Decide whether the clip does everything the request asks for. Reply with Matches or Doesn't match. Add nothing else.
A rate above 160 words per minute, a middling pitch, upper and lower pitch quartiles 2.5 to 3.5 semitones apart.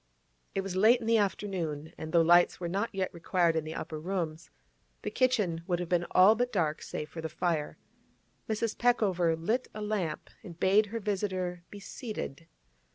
Doesn't match